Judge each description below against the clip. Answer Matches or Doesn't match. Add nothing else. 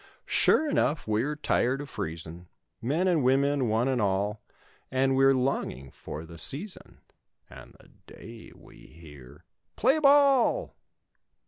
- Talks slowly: Matches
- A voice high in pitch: Doesn't match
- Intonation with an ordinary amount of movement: Doesn't match